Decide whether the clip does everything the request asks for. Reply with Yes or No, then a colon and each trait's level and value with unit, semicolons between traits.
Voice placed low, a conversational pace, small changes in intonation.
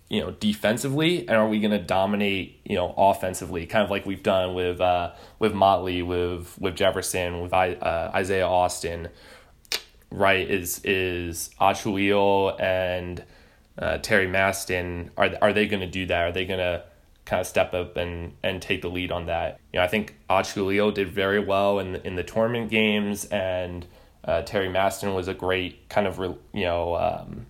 Yes: very low, 95 Hz; average, 185 wpm; narrow, 2.1 semitones